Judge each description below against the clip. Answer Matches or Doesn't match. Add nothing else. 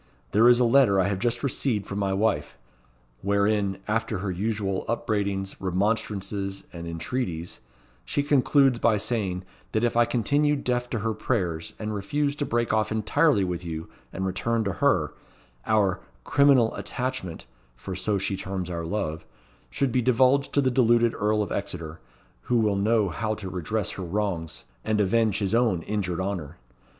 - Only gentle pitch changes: Doesn't match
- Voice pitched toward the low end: Matches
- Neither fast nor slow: Matches